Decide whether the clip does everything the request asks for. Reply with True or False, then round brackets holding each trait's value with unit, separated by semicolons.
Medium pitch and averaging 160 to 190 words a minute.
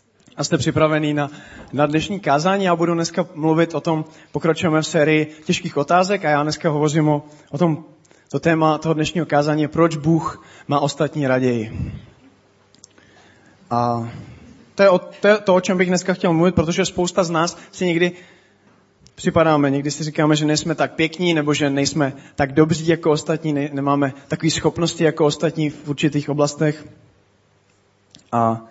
True (155 Hz; 165 wpm)